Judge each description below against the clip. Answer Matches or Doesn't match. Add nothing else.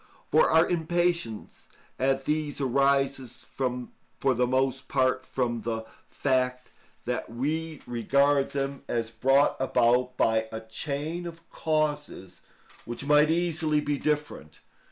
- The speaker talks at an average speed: Doesn't match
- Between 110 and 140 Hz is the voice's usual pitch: Matches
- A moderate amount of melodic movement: Matches